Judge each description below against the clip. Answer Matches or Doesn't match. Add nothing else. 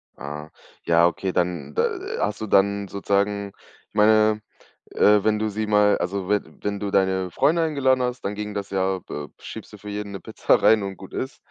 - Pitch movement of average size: Doesn't match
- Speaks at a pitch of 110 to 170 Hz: Doesn't match